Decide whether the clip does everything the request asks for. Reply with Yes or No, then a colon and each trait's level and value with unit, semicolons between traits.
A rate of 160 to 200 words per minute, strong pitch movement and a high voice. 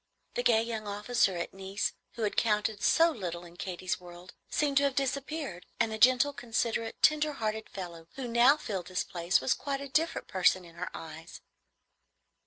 Yes: average, 185 wpm; wide, 6.4 semitones; high, 220 Hz